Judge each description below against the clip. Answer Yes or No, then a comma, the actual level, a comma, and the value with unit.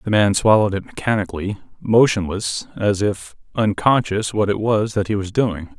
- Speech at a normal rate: Yes, average, 165 wpm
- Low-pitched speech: Yes, low, 105 Hz